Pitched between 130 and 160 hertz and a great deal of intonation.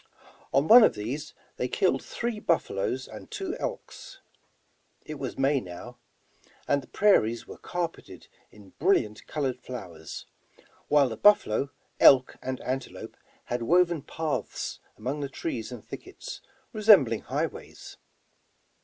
Yes: medium, 140 Hz; wide, 6.8 semitones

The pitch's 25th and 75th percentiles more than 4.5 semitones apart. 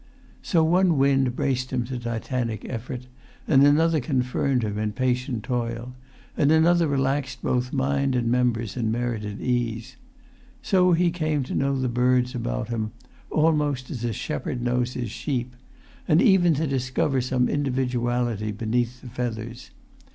No: narrow, 2.6 semitones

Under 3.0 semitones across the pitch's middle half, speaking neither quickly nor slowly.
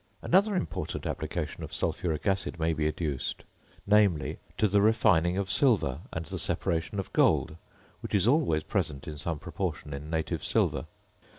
No: average, 5.1 semitones; average, 160 wpm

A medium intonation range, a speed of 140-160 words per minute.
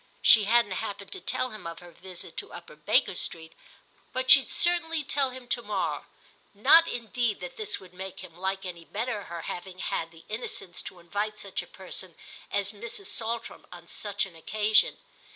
No: average, 4.8 semitones; average, 185 wpm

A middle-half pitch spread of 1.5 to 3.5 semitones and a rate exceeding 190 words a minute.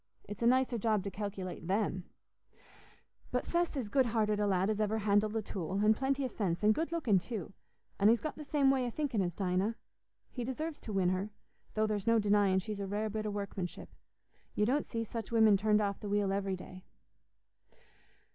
Yes: average, 2.9 semitones; fast, 205 wpm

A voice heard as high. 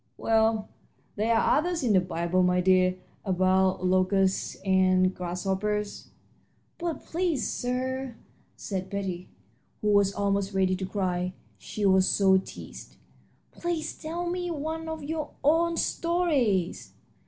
Yes: high, 200 Hz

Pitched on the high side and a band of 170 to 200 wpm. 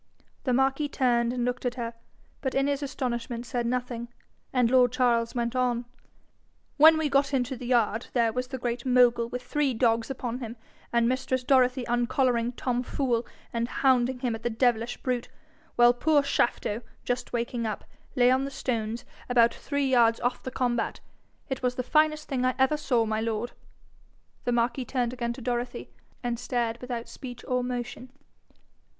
Yes: high, 245 Hz; average, 175 wpm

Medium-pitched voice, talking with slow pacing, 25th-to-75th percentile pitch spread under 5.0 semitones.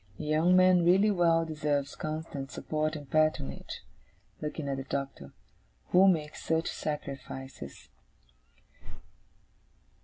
Yes: medium, 155 Hz; slow, 110 wpm; average, 3.0 semitones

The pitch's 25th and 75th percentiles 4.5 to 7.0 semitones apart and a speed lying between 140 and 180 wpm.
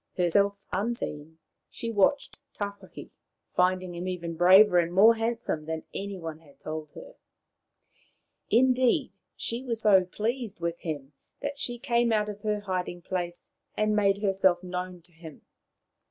No: average, 4.0 semitones; average, 145 wpm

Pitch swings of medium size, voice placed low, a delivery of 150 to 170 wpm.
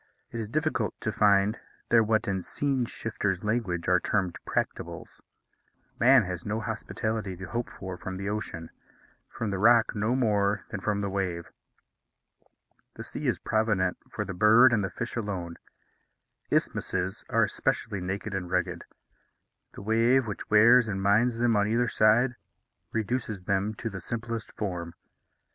Yes: average, 3.1 semitones; low, 105 Hz; average, 155 wpm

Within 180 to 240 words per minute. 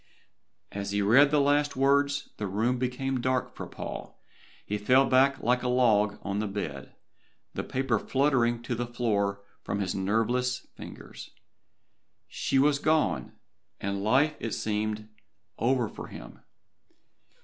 No: average, 140 wpm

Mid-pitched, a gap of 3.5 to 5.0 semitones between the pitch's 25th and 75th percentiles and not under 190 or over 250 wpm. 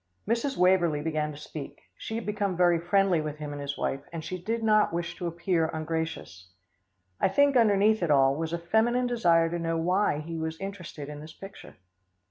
Yes: medium, 170 Hz; average, 4.1 semitones; fast, 205 wpm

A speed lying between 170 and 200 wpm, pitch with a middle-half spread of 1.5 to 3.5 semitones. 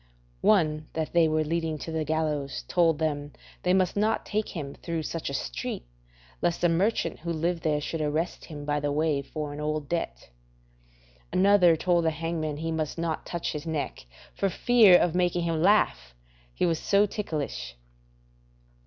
Yes: average, 175 wpm; narrow, 2.5 semitones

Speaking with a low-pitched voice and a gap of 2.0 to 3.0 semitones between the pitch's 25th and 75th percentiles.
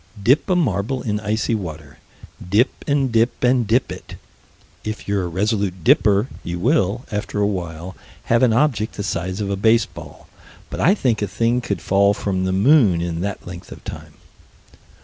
No: low, 105 Hz; average, 4.0 semitones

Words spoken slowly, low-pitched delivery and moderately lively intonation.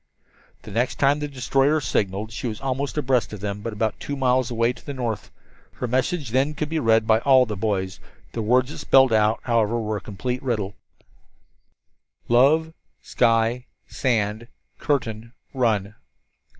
No: average, 165 wpm; low, 120 Hz; average, 3.5 semitones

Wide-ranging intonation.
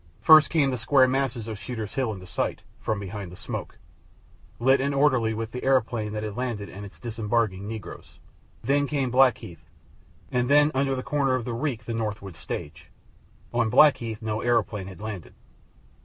No: average, 3.8 semitones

